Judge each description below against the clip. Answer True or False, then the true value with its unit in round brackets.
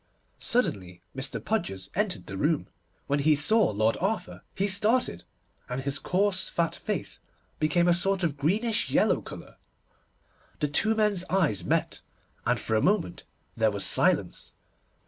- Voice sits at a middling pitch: True (170 Hz)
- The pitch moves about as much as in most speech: False (7.2 semitones)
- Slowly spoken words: False (145 wpm)